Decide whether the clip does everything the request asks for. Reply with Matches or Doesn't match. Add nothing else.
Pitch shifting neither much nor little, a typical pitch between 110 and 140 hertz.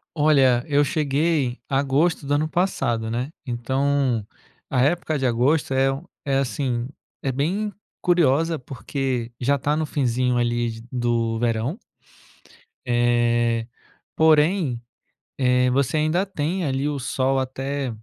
Matches